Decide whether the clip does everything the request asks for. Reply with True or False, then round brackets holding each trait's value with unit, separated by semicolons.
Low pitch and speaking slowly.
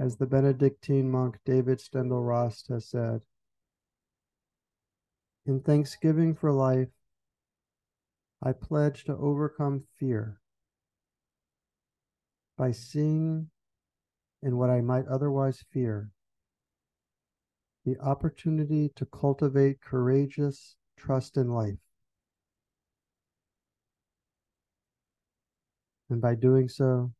True (130 Hz; 85 wpm)